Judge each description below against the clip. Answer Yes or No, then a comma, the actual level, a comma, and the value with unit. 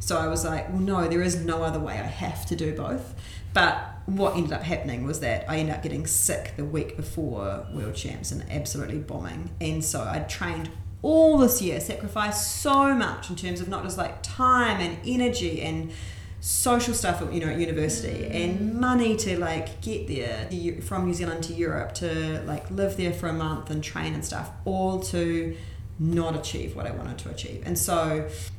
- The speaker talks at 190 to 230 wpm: Yes, average, 200 wpm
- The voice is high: No, low, 100 Hz